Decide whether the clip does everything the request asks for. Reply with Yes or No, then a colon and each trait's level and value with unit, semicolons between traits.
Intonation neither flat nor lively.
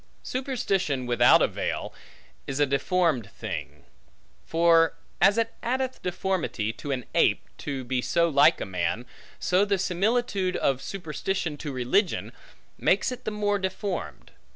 No: wide, 6.6 semitones